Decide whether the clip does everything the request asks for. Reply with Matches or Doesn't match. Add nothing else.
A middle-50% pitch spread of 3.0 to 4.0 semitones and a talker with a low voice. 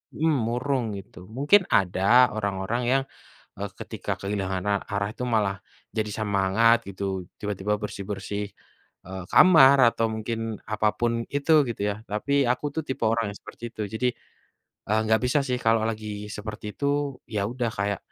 Matches